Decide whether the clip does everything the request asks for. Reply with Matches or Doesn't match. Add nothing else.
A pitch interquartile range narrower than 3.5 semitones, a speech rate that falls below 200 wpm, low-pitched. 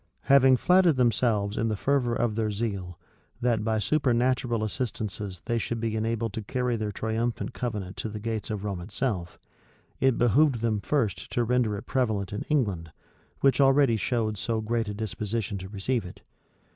Matches